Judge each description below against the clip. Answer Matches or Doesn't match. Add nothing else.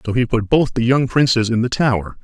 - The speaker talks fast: Matches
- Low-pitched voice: Matches